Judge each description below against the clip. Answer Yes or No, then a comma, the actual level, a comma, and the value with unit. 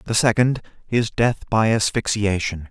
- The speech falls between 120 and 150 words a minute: Yes, slow, 135 wpm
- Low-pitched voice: Yes, low, 110 Hz